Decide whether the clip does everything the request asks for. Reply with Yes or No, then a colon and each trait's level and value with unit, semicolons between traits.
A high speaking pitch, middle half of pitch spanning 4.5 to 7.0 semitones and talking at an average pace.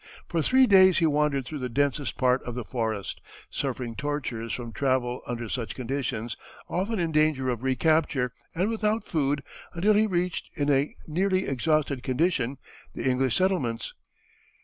No: medium, 140 Hz; average, 5.1 semitones; average, 155 wpm